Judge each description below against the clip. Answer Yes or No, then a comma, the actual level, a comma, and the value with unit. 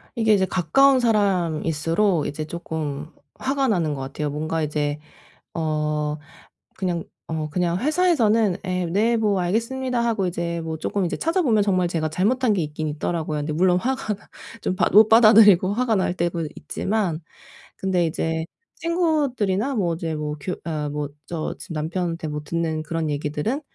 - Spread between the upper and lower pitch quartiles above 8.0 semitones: No, wide, 5.6 semitones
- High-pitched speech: No, medium, 175 Hz